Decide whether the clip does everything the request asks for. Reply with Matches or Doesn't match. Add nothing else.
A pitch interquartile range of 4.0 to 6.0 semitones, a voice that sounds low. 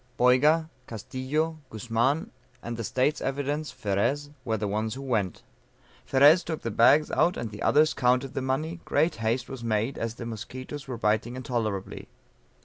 Matches